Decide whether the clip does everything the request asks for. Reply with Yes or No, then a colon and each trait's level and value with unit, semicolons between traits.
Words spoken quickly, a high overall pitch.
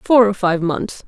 Yes: fast, 225 wpm; high, 195 Hz